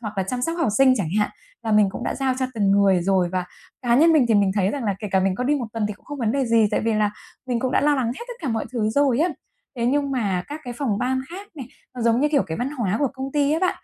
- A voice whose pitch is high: Yes, high, 240 Hz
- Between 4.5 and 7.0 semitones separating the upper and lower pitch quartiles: Yes, average, 5.0 semitones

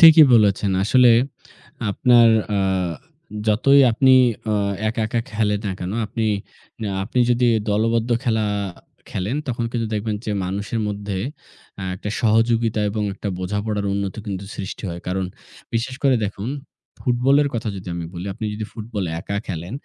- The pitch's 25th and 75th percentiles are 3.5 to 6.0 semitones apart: No, average, 2.8 semitones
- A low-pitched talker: Yes, low, 110 Hz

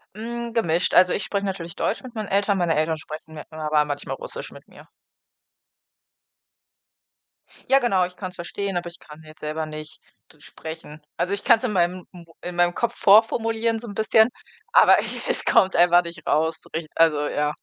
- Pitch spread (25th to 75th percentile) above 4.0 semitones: Yes, average, 5.2 semitones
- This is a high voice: No, medium, 175 Hz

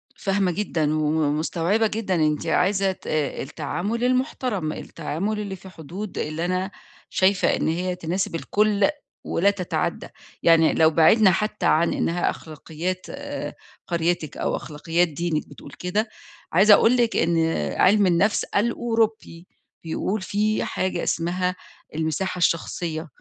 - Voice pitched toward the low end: No, medium, 180 Hz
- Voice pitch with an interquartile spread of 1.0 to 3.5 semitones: No, average, 4.0 semitones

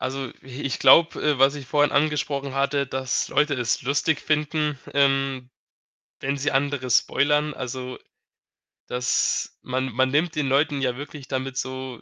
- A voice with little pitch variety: Yes, narrow, 2.1 semitones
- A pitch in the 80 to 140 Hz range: Yes, low, 135 Hz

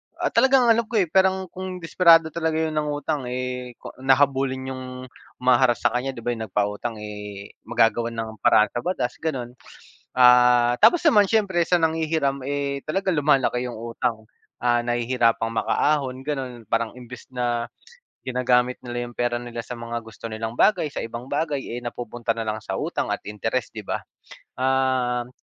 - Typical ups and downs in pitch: Yes, average, 3.8 semitones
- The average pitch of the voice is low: Yes, low, 125 Hz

